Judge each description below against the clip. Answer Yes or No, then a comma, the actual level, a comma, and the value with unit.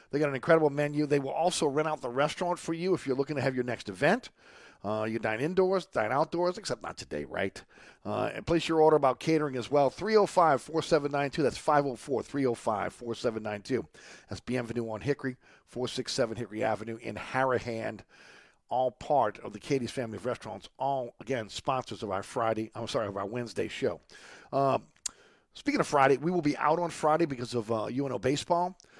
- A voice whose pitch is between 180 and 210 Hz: No, low, 135 Hz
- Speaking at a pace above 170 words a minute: Yes, average, 185 wpm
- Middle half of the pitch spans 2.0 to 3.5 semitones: No, average, 4.7 semitones